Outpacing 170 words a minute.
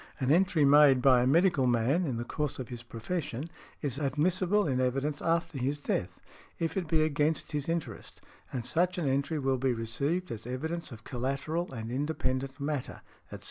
Yes: average, 180 wpm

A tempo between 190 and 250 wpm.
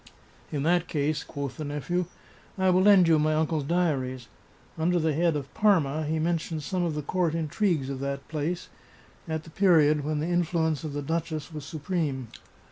Yes: average, 200 wpm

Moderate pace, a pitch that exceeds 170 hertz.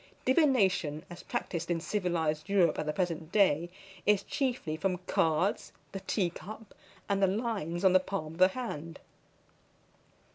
Yes: average, 150 wpm; medium, 185 Hz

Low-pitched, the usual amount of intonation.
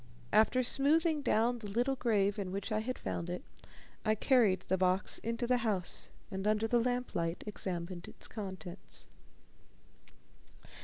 No: high, 215 Hz; average, 4.4 semitones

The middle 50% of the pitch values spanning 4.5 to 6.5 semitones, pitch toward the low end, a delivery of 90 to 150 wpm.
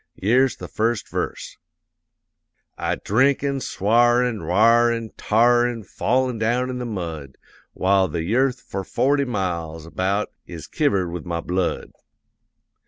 Yes: average, 5.1 semitones; low, 110 Hz; average, 140 wpm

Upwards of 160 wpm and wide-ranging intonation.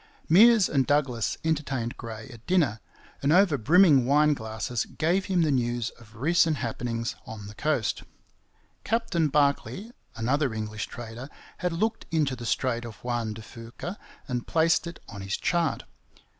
No: average, 155 wpm; wide, 6.0 semitones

